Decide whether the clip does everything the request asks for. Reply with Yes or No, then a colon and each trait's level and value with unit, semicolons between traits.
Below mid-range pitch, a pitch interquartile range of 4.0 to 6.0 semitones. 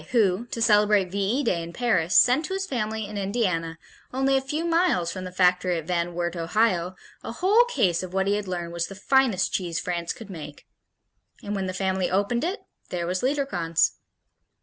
No: high, 195 Hz; wide, 5.4 semitones